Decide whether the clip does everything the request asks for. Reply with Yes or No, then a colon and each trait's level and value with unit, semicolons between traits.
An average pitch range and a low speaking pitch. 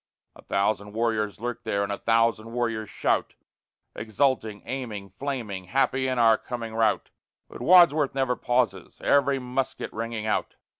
Yes: average, 3.3 semitones; low, 115 Hz